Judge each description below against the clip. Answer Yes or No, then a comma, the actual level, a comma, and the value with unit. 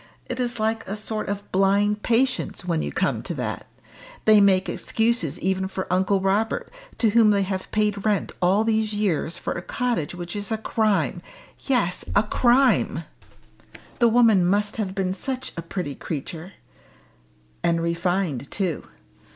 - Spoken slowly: No, average, 160 wpm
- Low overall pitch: No, high, 200 Hz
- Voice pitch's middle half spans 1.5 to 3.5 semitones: Yes, average, 3.2 semitones